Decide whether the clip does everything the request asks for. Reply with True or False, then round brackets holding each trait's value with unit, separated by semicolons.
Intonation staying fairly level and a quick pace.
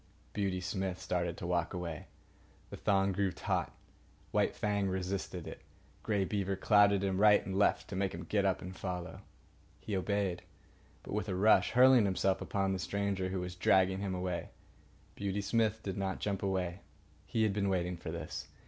False (1.7 semitones; 180 wpm)